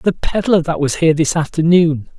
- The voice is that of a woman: No, male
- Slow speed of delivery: No, average, 190 wpm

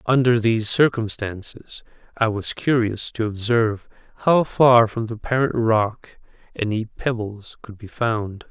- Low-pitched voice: Yes, low, 115 Hz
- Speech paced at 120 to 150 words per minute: Yes, slow, 135 wpm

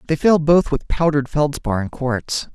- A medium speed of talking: Yes, average, 190 wpm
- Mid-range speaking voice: Yes, medium, 145 Hz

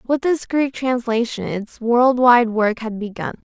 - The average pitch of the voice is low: No, high, 240 Hz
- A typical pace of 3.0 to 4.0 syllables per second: Yes, 3.9 syllables/s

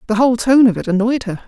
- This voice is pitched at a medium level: No, high, 230 Hz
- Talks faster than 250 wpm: Yes, fast, 285 wpm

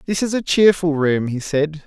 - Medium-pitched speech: Yes, medium, 165 Hz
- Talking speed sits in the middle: No, fast, 225 wpm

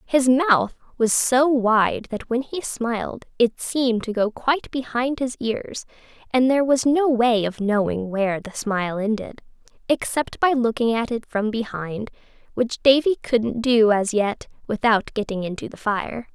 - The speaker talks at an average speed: Yes, average, 170 wpm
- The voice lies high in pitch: Yes, high, 235 Hz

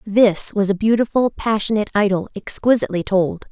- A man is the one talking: No, female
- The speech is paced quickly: No, slow, 135 wpm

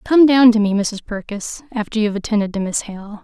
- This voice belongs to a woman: Yes, female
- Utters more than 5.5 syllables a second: Yes, 5.7 syllables/s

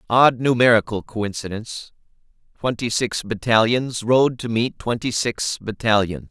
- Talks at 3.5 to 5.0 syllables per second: Yes, 4.4 syllables/s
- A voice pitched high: No, low, 115 Hz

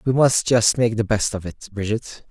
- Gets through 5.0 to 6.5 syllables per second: No, 4.7 syllables/s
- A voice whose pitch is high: No, low, 115 Hz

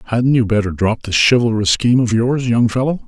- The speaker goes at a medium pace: No, fast, 215 wpm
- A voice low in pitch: Yes, low, 115 Hz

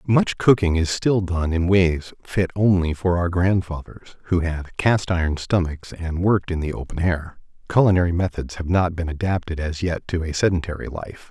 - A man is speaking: Yes, male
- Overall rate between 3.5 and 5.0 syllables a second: Yes, 4.9 syllables/s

